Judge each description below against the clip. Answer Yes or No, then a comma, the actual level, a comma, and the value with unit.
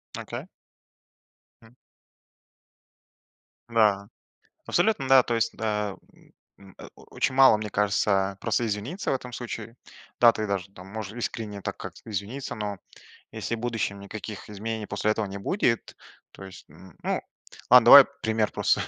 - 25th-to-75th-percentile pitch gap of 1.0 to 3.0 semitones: Yes, narrow, 2.6 semitones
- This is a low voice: Yes, low, 110 Hz